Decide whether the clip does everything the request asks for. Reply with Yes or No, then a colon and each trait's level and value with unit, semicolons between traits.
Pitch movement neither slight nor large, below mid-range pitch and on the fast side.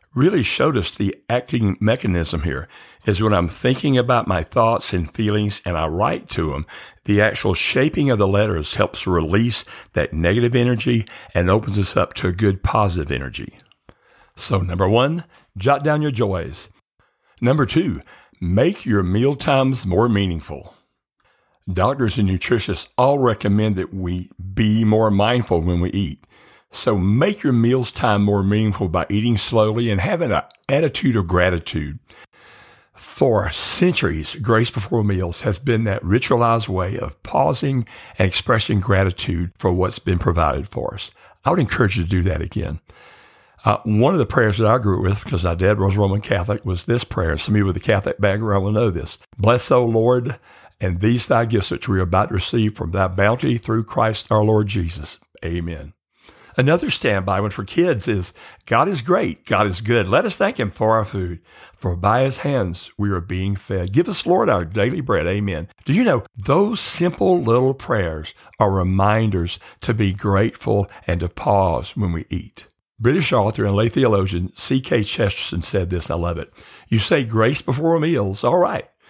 No: average, 4.1 semitones; low, 100 Hz; average, 180 wpm